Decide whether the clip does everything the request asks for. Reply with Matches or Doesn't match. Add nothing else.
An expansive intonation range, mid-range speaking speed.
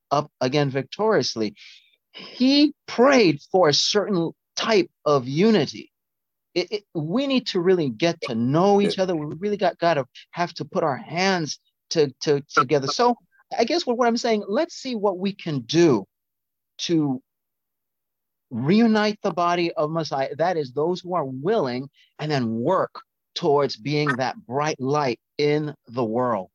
Matches